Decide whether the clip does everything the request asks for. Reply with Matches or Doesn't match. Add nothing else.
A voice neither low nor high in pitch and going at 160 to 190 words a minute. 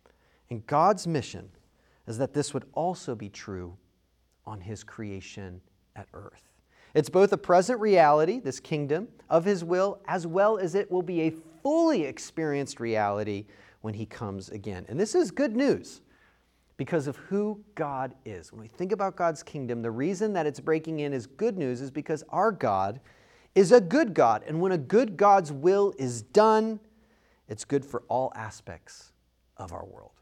Matches